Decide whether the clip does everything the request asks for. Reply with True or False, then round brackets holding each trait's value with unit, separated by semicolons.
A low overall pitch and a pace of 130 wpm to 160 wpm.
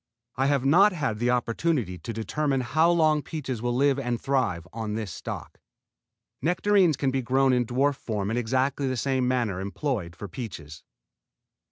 False (130 Hz; 170 wpm)